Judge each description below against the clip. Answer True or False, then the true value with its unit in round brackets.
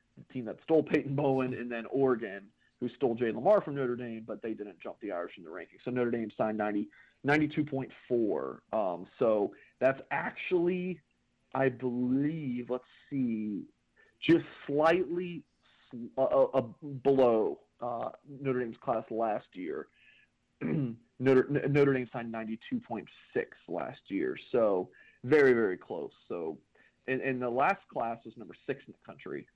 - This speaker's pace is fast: False (150 wpm)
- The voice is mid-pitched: False (130 Hz)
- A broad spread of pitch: False (4.2 semitones)